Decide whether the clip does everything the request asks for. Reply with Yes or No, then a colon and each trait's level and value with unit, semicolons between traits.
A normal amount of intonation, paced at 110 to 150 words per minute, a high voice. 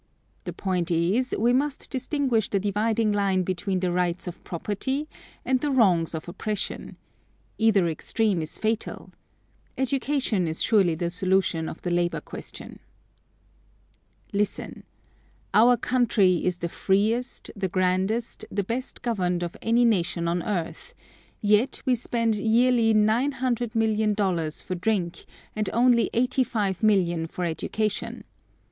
Yes: average, 4.5 semitones; slow, 135 wpm; high, 210 Hz